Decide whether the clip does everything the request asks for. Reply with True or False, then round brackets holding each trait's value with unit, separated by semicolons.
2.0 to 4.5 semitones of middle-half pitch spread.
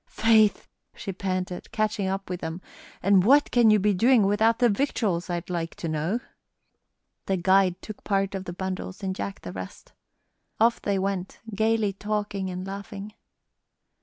True (2.5 semitones)